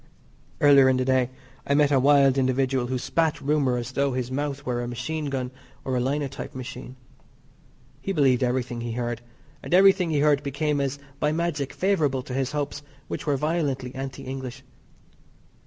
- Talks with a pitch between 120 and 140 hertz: Yes, low, 135 Hz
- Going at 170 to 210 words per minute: Yes, average, 175 wpm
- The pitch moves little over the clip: Yes, narrow, 2.3 semitones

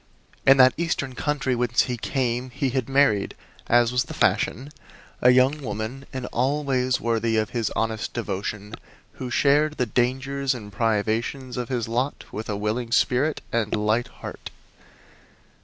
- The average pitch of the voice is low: Yes, low, 125 Hz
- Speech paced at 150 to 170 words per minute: Yes, average, 155 wpm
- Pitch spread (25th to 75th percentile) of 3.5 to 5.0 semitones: No, average, 3.0 semitones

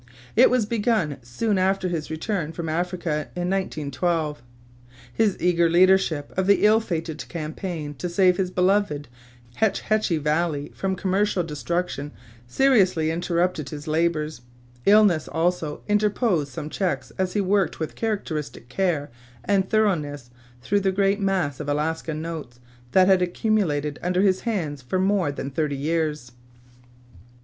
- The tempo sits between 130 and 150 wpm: Yes, average, 140 wpm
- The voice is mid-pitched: Yes, medium, 175 Hz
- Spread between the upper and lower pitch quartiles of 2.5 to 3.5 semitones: No, average, 4.2 semitones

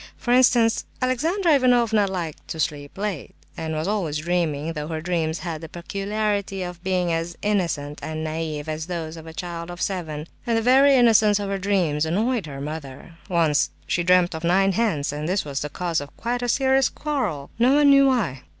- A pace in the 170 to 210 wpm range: Yes, average, 195 wpm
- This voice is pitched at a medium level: Yes, medium, 175 Hz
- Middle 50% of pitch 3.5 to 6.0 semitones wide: Yes, wide, 5.6 semitones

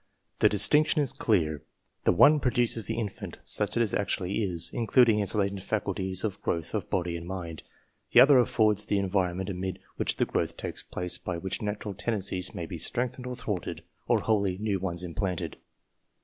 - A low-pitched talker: Yes, low, 100 Hz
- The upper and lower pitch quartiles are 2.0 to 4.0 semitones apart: Yes, average, 3.4 semitones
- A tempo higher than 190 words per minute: No, average, 185 wpm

